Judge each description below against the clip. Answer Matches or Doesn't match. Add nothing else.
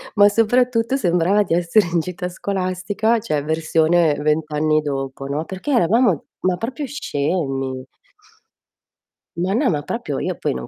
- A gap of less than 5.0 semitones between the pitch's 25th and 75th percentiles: Doesn't match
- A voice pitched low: Doesn't match